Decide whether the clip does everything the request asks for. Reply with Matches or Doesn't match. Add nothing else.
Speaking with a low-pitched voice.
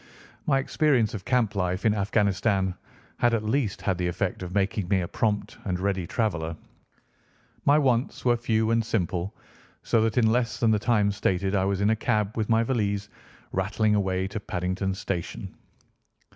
Matches